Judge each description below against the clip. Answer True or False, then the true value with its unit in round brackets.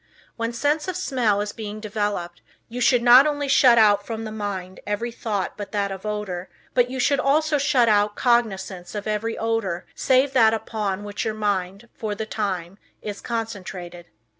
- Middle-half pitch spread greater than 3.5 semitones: False (3.1 semitones)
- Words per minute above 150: True (180 wpm)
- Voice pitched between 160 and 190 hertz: False (215 Hz)